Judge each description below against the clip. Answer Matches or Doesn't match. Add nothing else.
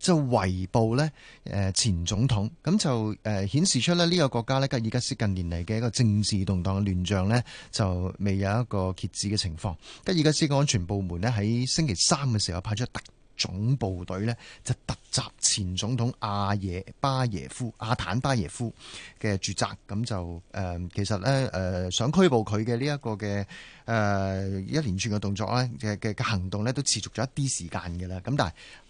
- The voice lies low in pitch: Matches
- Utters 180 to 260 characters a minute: Doesn't match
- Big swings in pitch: Doesn't match